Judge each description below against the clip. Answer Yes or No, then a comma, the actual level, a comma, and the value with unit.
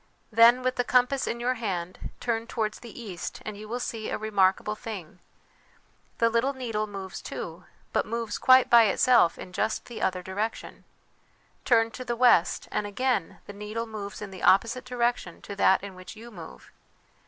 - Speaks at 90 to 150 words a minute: No, average, 185 wpm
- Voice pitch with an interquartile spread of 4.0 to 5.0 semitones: No, average, 3.2 semitones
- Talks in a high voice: Yes, high, 220 Hz